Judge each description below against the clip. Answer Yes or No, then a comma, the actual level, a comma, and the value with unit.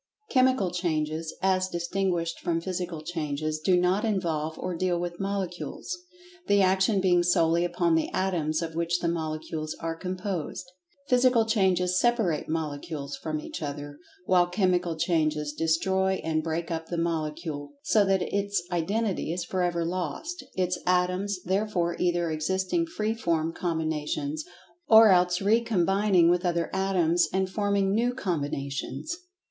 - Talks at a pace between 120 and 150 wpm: Yes, average, 140 wpm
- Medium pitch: Yes, medium, 175 Hz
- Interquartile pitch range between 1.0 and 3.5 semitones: Yes, average, 2.9 semitones